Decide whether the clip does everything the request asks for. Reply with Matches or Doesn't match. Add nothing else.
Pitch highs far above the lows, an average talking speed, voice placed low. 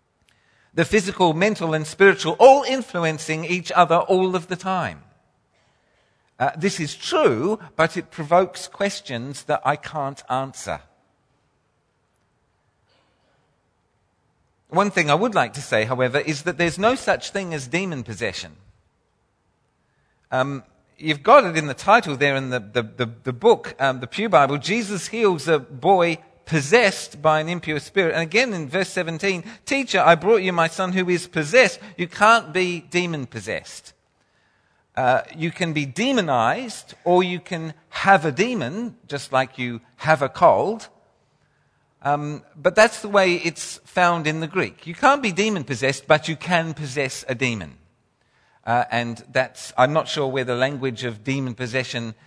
Doesn't match